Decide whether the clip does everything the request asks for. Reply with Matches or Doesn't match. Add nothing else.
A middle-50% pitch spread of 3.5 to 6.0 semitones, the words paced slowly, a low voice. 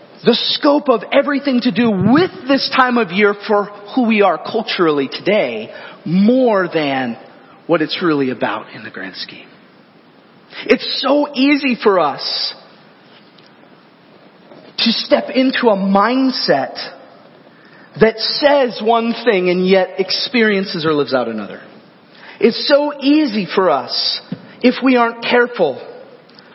Doesn't match